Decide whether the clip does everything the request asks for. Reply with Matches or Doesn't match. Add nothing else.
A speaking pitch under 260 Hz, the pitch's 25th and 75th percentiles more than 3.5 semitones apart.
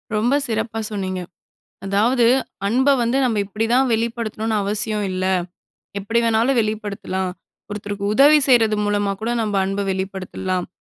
Doesn't match